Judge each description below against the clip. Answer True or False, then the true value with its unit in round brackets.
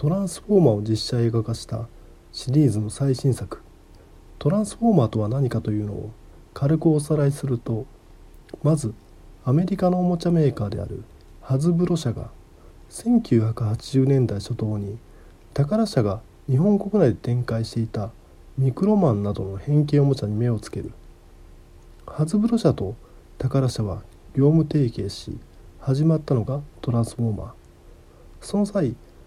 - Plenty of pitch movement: True (6.3 semitones)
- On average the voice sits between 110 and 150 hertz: True (115 Hz)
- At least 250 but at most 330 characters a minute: True (310 characters per minute)